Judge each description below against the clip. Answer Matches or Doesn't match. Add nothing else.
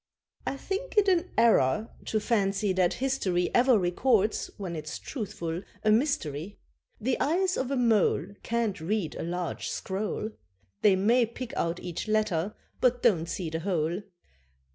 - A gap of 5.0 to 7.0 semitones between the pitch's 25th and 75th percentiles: Matches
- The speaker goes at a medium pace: Matches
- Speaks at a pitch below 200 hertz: Doesn't match